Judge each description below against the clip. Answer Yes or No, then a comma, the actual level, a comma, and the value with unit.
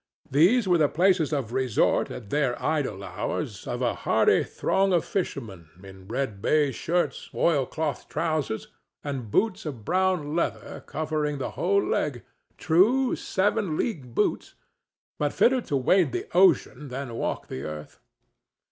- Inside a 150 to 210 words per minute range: No, average, 140 wpm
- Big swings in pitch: Yes, wide, 6.0 semitones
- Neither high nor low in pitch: Yes, medium, 150 Hz